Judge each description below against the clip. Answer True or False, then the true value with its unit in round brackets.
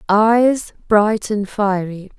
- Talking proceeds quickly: False (80 wpm)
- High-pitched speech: True (210 Hz)